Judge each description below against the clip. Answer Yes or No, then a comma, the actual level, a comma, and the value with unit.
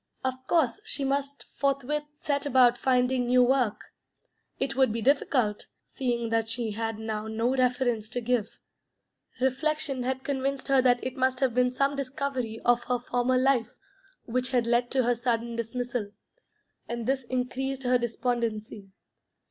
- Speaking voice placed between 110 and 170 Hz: No, very high, 250 Hz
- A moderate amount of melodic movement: No, narrow, 2.1 semitones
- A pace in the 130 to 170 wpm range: Yes, average, 155 wpm